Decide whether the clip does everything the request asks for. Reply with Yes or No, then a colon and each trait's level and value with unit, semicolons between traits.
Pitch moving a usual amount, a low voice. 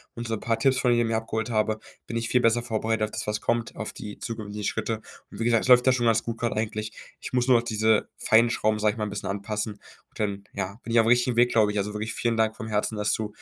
No: narrow, 1.7 semitones; low, 110 Hz